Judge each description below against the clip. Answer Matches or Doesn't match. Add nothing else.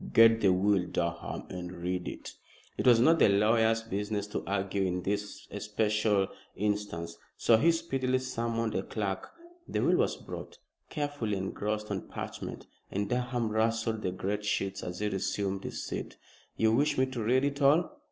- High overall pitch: Doesn't match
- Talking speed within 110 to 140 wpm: Doesn't match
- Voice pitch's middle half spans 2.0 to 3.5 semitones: Matches